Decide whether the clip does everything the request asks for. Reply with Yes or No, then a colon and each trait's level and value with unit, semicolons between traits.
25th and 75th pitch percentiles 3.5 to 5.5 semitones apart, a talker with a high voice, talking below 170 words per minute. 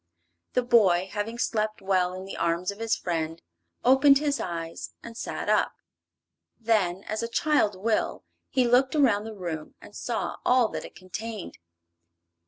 Yes: average, 4.4 semitones; high, 215 Hz; average, 160 wpm